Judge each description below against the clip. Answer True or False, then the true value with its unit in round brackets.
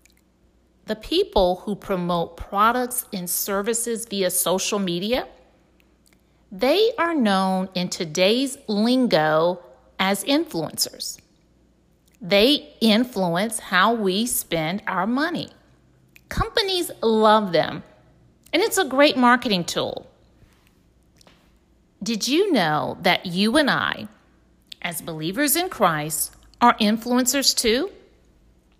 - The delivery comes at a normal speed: False (100 wpm)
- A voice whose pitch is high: True (210 Hz)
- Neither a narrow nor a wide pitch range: False (5.9 semitones)